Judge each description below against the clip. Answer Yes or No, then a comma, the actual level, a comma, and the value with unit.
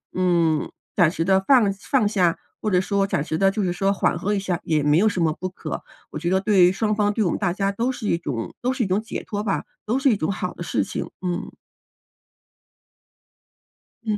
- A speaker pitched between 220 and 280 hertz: No, high, 195 Hz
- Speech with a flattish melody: No, average, 3.3 semitones